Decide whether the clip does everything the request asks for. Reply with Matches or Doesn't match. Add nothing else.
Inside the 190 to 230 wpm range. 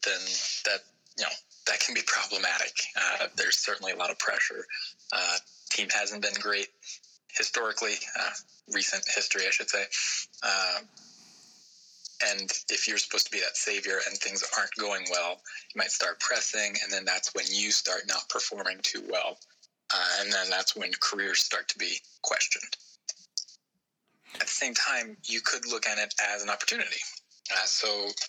Doesn't match